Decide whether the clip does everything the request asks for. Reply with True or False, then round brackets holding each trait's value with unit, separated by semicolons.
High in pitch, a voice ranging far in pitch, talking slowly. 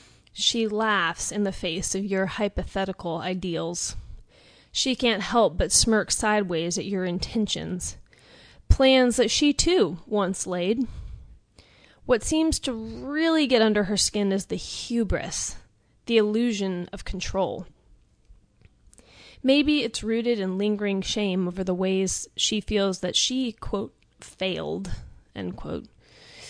False (205 Hz; 4.0 semitones; 125 wpm)